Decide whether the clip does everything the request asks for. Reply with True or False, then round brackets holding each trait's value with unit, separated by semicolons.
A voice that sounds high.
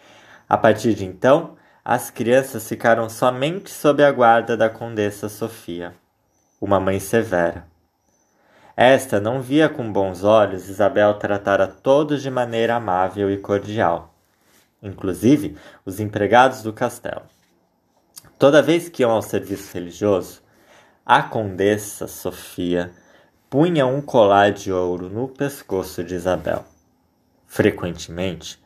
False (105 Hz)